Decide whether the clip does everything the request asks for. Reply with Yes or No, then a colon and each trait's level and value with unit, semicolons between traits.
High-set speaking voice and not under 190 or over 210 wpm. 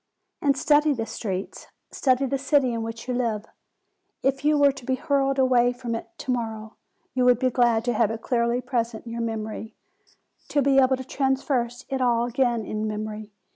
Yes: high, 245 Hz; average, 200 wpm